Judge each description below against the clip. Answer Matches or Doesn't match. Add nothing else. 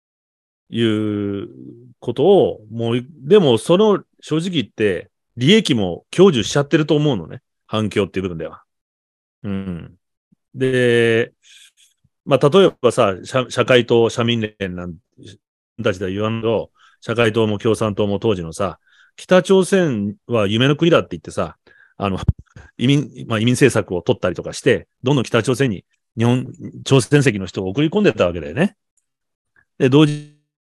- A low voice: Matches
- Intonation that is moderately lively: Doesn't match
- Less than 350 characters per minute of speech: Matches